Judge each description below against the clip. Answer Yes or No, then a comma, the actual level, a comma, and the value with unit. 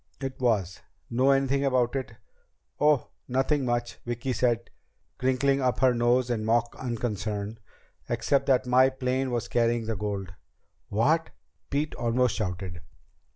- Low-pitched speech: Yes, low, 125 Hz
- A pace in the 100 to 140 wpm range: Yes, slow, 135 wpm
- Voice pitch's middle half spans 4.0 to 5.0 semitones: No, narrow, 2.6 semitones